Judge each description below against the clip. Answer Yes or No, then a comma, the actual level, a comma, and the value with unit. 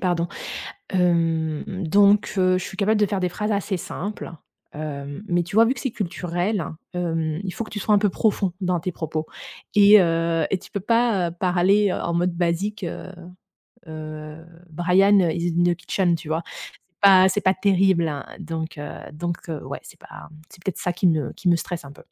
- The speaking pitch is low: No, medium, 180 Hz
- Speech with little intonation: No, average, 3.0 semitones